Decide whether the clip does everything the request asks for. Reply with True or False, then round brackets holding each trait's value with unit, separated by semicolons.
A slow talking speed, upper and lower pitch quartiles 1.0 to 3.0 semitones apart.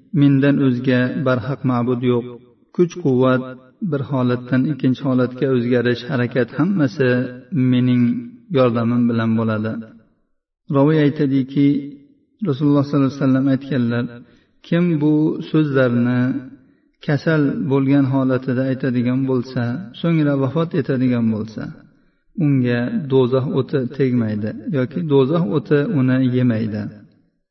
True (100 wpm; 2.4 semitones)